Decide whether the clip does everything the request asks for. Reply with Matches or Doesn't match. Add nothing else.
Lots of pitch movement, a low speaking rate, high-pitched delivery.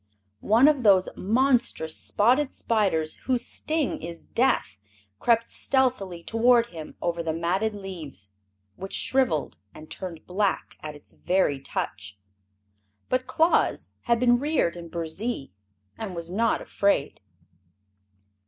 Matches